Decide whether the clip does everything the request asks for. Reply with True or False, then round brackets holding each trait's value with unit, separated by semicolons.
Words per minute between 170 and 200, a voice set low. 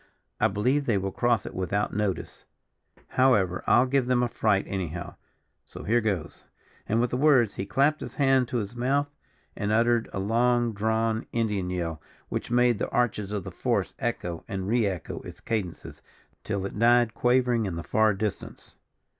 True (180 wpm; 110 Hz)